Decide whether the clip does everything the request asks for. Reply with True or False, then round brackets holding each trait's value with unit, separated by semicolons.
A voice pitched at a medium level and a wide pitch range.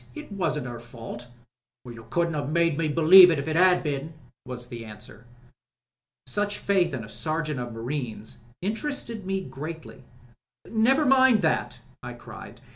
True (155 Hz; 7.2 semitones)